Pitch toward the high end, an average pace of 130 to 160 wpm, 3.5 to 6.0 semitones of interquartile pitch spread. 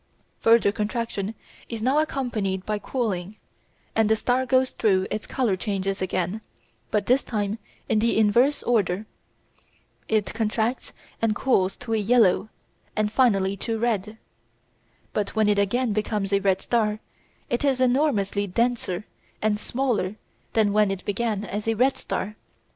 No: high, 215 Hz; average, 145 wpm; average, 2.9 semitones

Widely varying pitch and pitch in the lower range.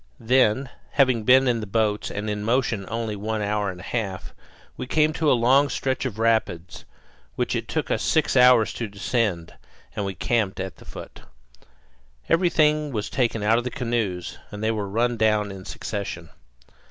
No: average, 3.6 semitones; low, 110 Hz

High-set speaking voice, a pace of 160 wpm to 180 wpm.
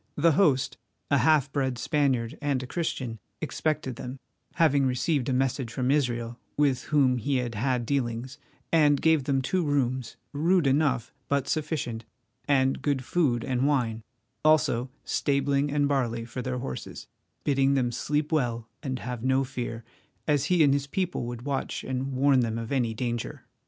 No: low, 135 Hz; average, 165 wpm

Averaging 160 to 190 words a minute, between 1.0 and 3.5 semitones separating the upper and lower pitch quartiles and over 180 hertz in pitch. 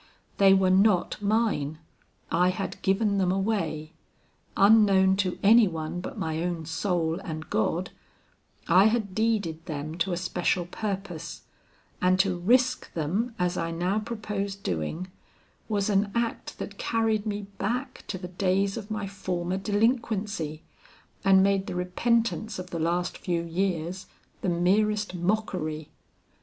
No: average, 140 wpm; average, 3.2 semitones; high, 190 Hz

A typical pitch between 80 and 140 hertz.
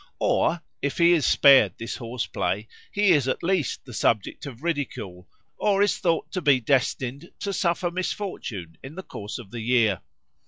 Yes: low, 135 Hz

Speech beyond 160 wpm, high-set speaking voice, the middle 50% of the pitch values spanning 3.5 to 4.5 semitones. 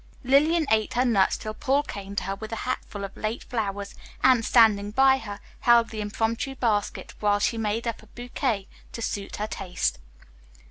No: average, 185 wpm; high, 220 Hz; average, 3.1 semitones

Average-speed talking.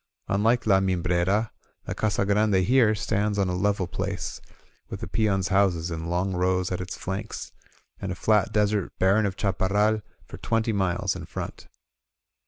Yes: average, 165 wpm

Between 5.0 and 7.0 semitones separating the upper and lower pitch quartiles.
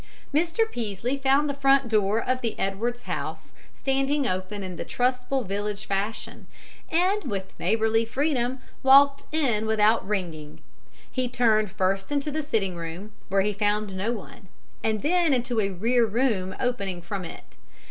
Yes: average, 5.3 semitones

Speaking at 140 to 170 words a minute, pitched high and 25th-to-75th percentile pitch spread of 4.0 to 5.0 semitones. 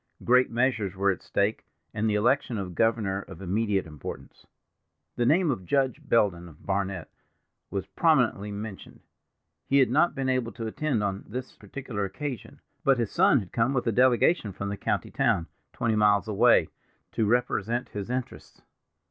No: average, 165 wpm; low, 110 Hz; average, 4.3 semitones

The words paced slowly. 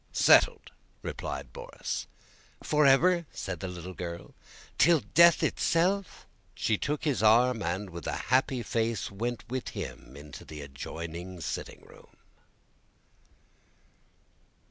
Yes: slow, 115 wpm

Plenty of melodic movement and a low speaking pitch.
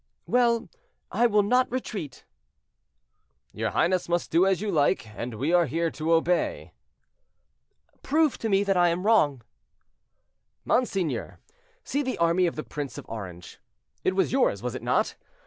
No: wide, 6.1 semitones; medium, 175 Hz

